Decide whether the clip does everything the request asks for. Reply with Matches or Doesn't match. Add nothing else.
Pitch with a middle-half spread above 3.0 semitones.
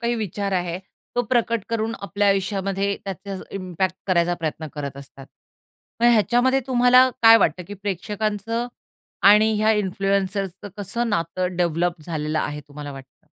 Matches